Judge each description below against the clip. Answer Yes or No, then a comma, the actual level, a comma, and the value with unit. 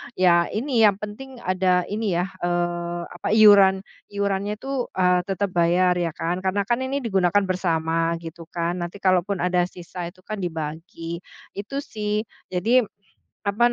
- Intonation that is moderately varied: Yes, average, 3.0 semitones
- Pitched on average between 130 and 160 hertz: No, medium, 185 Hz